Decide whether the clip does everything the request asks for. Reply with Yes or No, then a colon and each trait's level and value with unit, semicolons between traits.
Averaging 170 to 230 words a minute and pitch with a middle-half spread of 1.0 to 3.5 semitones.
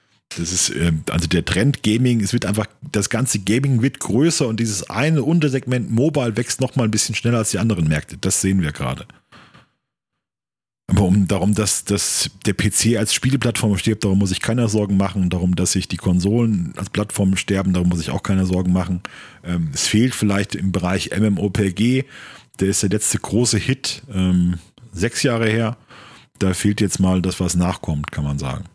No: average, 185 wpm; average, 3.9 semitones